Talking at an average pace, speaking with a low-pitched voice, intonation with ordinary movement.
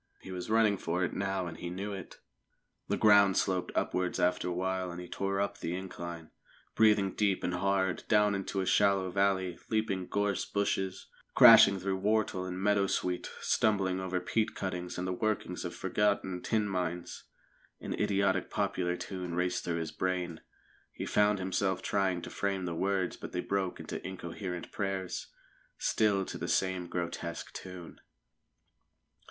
No: average, 160 wpm; very low, 95 Hz; narrow, 1.7 semitones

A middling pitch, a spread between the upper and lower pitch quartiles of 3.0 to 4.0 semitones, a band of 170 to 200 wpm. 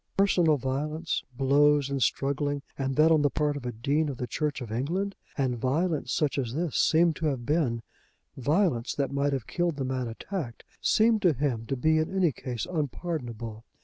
Yes: medium, 145 Hz; average, 3.7 semitones; average, 190 wpm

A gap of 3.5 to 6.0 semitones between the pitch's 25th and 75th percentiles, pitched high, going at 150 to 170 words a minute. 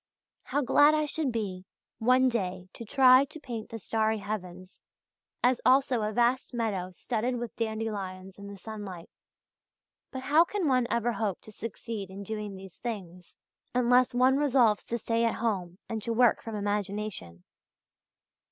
Yes: average, 3.8 semitones; high, 225 Hz; average, 160 wpm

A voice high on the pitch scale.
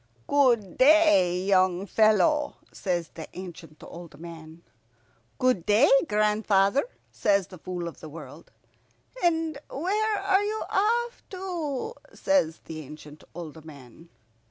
Yes: high, 200 Hz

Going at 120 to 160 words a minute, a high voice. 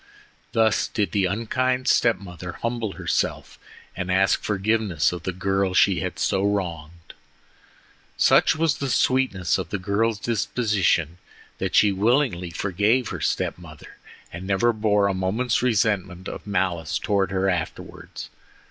No: average, 140 wpm; low, 100 Hz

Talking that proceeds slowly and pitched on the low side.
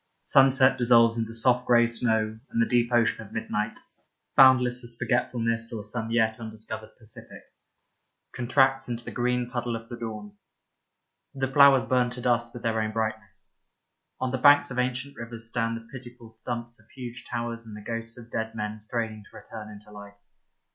No: average, 175 wpm; low, 115 Hz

